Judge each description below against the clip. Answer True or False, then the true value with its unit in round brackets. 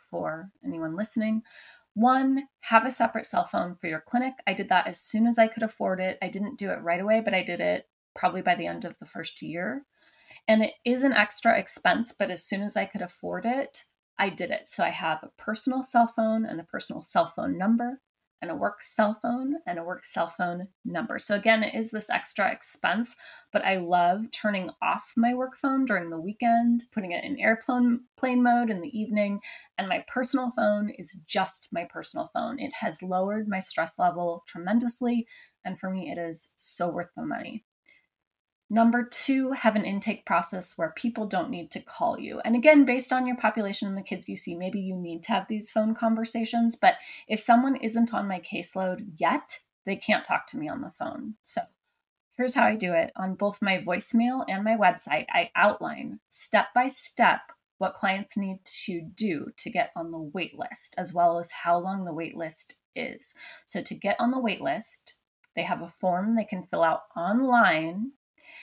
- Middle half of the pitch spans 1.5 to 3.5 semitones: False (4.4 semitones)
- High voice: True (215 Hz)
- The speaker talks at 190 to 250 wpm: True (205 wpm)